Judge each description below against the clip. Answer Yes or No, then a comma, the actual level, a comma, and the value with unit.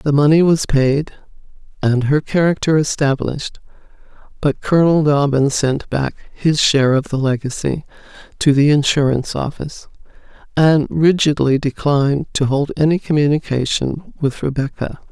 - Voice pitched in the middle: Yes, medium, 145 Hz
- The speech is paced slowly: Yes, slow, 125 wpm